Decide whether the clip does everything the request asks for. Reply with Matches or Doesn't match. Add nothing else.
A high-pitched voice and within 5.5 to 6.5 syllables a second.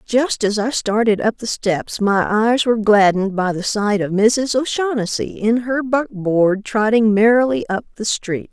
Doesn't match